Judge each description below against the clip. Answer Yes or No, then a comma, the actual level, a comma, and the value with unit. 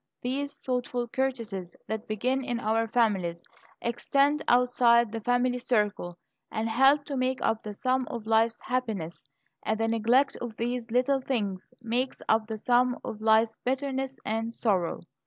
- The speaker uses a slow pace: No, average, 155 wpm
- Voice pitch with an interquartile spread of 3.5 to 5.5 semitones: No, narrow, 2.6 semitones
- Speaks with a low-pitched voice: No, high, 235 Hz